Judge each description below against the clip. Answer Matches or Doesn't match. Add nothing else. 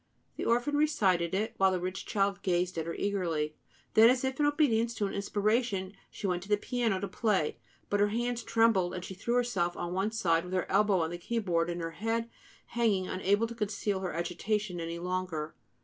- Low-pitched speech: Doesn't match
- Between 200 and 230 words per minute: Matches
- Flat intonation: Doesn't match